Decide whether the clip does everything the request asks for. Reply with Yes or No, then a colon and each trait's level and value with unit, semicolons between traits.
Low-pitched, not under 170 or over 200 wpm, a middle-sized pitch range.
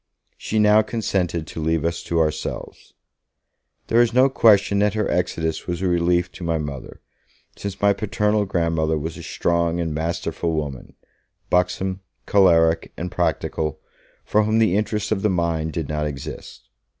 No: very low, 85 Hz; average, 160 wpm; average, 4.0 semitones